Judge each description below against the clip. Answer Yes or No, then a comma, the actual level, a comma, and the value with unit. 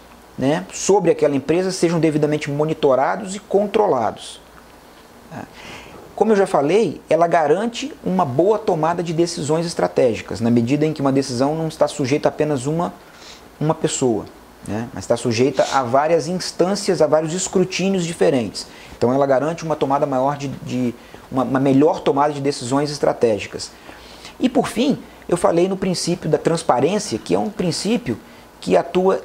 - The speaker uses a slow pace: No, average, 160 wpm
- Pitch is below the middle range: No, medium, 155 Hz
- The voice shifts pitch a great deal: No, average, 4.5 semitones